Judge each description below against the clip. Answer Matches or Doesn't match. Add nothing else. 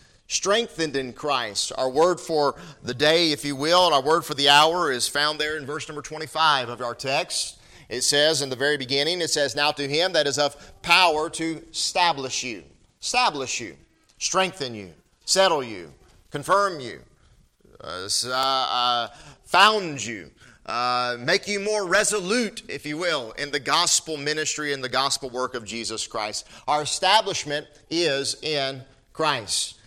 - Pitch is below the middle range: Doesn't match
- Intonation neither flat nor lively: Matches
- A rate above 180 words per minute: Doesn't match